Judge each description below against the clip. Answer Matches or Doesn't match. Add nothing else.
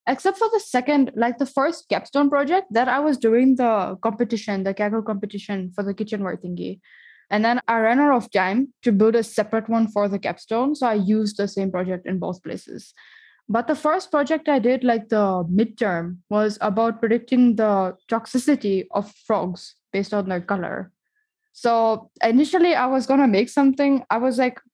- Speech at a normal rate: Matches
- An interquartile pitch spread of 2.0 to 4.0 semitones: Doesn't match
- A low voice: Doesn't match